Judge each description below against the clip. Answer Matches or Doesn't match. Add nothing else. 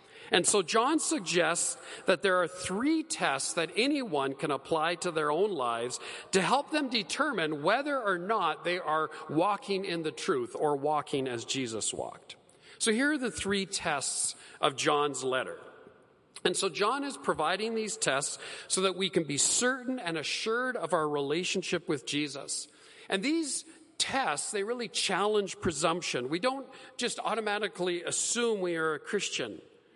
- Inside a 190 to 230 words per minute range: Doesn't match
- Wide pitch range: Matches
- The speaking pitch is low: Doesn't match